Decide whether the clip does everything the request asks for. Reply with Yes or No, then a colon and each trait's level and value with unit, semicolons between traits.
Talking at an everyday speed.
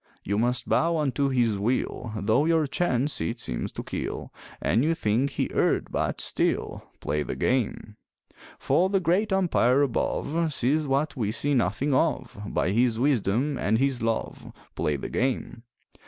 Yes: average, 160 wpm